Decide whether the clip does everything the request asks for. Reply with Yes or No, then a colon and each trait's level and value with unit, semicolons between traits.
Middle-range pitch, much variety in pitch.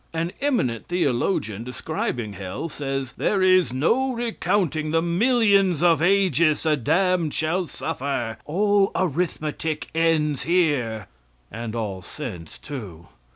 Yes: medium, 160 Hz; wide, 6.4 semitones